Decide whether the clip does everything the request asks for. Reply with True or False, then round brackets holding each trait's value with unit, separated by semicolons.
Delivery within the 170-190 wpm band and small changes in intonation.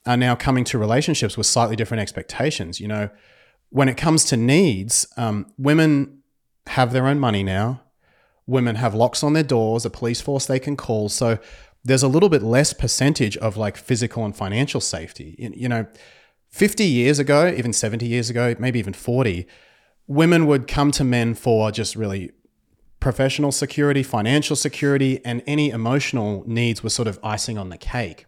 False (175 wpm; 4.0 semitones)